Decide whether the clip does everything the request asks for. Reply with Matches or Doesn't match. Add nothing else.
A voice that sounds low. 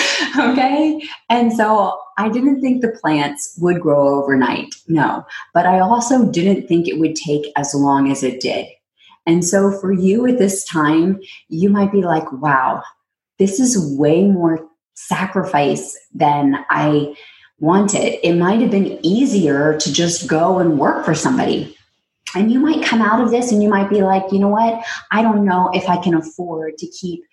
Doesn't match